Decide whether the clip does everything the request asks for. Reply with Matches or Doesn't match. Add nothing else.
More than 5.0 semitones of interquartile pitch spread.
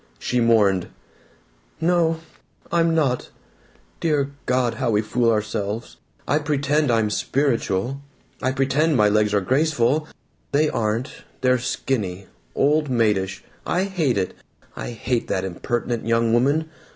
Matches